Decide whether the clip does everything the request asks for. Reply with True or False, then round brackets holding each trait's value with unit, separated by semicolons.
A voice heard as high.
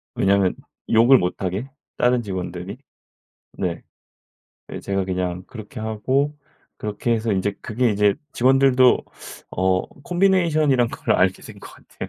False (110 Hz)